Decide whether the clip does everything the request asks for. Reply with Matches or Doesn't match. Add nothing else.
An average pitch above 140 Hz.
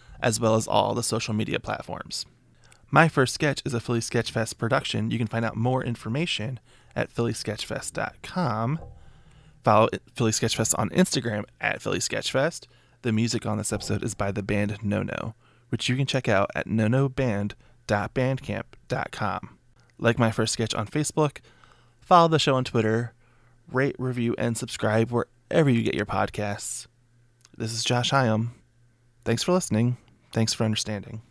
Doesn't match